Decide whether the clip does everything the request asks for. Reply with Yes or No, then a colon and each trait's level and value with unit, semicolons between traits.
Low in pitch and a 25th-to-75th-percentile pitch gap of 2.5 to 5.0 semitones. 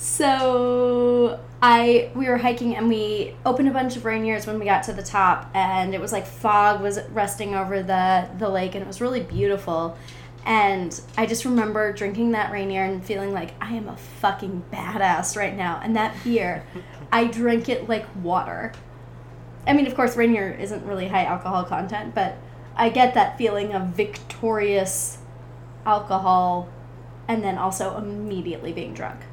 No: high, 205 Hz; average, 3.7 semitones